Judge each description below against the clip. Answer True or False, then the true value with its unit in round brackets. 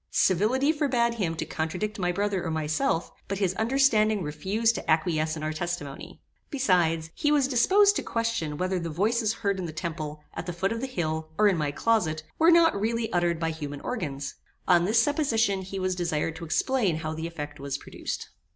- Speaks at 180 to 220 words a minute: True (195 wpm)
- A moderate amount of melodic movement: False (6.2 semitones)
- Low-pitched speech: False (185 Hz)